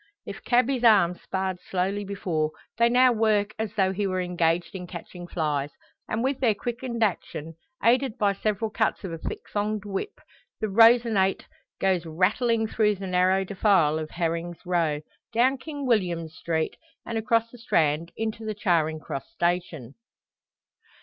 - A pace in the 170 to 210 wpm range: No, average, 155 wpm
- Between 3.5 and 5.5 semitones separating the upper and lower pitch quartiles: Yes, average, 4.6 semitones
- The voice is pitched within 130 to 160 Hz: No, high, 195 Hz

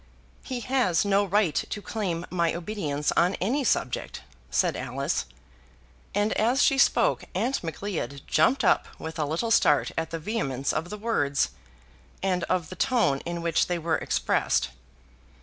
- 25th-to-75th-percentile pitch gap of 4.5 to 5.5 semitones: Yes, average, 5.2 semitones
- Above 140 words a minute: Yes, average, 155 wpm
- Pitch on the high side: No, medium, 180 Hz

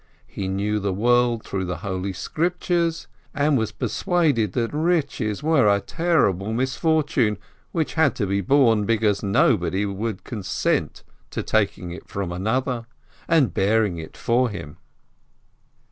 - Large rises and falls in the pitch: Yes, wide, 6.3 semitones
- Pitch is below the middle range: Yes, low, 110 Hz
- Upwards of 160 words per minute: No, average, 140 wpm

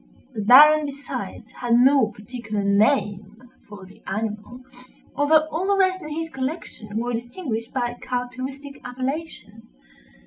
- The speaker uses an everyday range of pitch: Yes, average, 4.8 semitones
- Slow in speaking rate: Yes, slow, 130 wpm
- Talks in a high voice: Yes, very high, 250 Hz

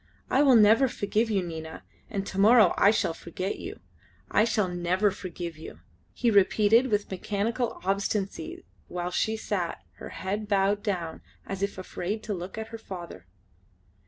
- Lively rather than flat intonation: No, average, 3.3 semitones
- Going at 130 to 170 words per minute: Yes, average, 160 wpm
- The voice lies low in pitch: No, high, 200 Hz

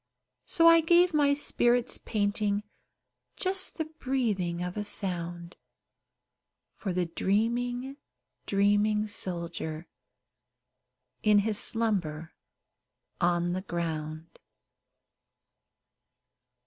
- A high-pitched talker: Yes, high, 205 Hz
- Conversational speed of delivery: No, slow, 85 wpm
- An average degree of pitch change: No, wide, 6.0 semitones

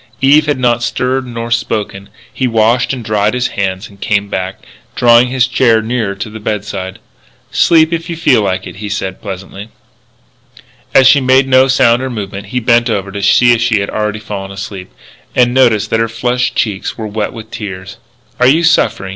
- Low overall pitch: Yes, low, 115 Hz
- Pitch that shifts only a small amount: No, average, 3.9 semitones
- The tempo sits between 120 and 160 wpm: No, average, 195 wpm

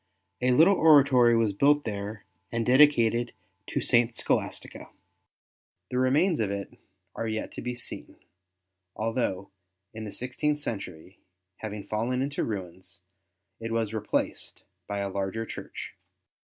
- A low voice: Yes, low, 115 Hz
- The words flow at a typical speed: No, slow, 130 wpm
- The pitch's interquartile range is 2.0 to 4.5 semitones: Yes, average, 3.9 semitones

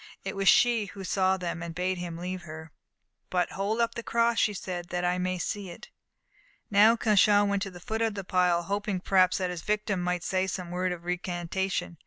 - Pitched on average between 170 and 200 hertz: Yes, medium, 185 Hz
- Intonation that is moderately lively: No, narrow, 2.3 semitones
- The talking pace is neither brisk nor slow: No, fast, 215 wpm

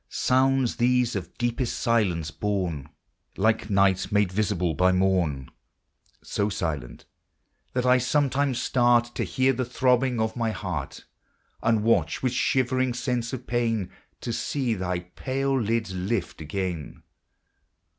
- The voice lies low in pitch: Yes, low, 115 Hz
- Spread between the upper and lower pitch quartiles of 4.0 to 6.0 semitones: Yes, average, 5.2 semitones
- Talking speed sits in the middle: No, slow, 130 wpm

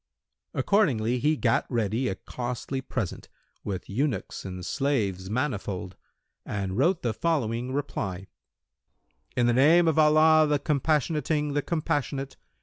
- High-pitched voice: No, low, 130 Hz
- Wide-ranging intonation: Yes, wide, 5.7 semitones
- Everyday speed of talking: No, slow, 125 wpm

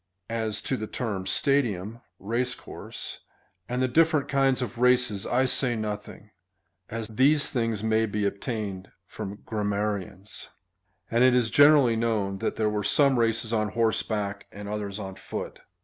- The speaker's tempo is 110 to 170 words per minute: Yes, average, 150 wpm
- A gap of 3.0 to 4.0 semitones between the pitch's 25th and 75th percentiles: Yes, average, 3.3 semitones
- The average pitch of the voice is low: Yes, low, 110 Hz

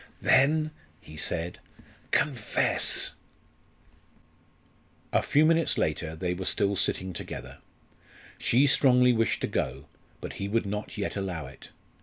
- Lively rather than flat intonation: Yes, wide, 7.1 semitones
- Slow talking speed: Yes, slow, 125 wpm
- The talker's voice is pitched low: Yes, low, 100 Hz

